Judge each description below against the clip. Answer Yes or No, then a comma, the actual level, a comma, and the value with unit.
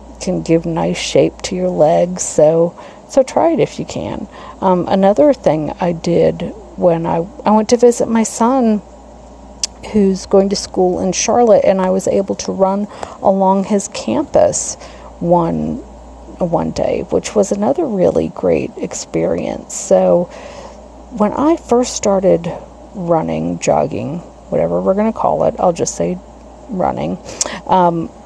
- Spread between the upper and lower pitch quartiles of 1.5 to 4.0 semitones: No, average, 4.7 semitones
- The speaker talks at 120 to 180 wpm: Yes, average, 145 wpm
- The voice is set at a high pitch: Yes, high, 195 Hz